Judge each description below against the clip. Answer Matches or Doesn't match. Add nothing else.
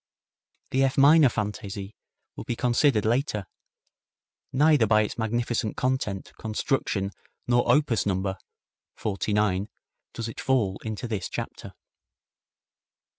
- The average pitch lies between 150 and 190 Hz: Doesn't match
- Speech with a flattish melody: Doesn't match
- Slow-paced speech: Matches